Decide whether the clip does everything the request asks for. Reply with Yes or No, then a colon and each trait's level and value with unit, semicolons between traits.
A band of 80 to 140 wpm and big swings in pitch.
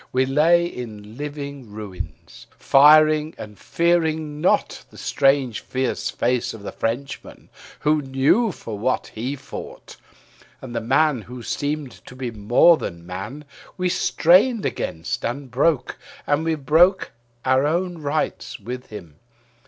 No: slow, 135 wpm; average, 4.5 semitones